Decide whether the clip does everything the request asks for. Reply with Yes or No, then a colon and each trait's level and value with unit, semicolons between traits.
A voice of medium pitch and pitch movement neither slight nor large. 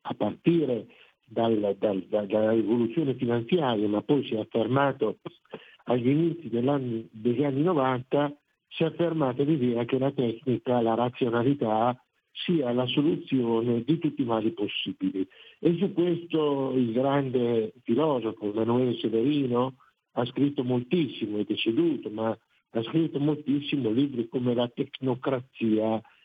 No: low, 125 Hz; average, 4.0 semitones